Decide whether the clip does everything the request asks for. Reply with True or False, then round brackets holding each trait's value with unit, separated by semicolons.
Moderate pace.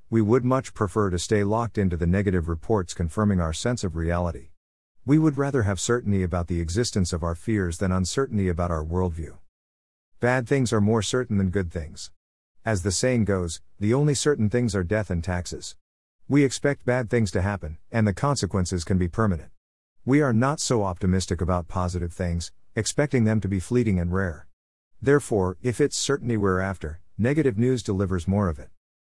True (190 wpm)